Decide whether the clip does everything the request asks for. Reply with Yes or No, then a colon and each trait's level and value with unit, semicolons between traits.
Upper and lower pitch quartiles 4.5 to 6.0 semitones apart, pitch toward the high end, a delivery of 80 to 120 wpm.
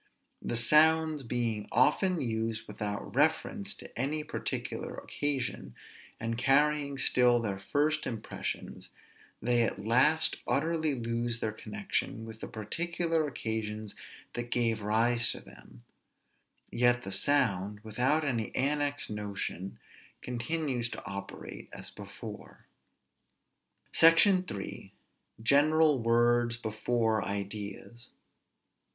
No: average, 5.1 semitones; low, 120 Hz; slow, 105 wpm